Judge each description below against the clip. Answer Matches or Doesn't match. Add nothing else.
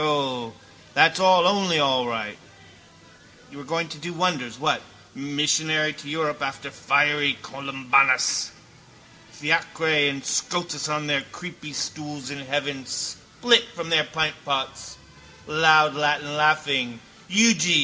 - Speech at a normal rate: Doesn't match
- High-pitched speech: Doesn't match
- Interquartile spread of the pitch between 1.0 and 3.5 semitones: Matches